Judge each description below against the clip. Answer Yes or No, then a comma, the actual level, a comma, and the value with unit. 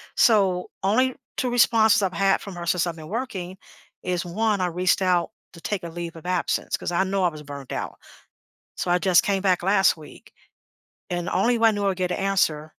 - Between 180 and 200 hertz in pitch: Yes, medium, 185 Hz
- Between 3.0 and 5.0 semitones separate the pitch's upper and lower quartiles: No, narrow, 2.6 semitones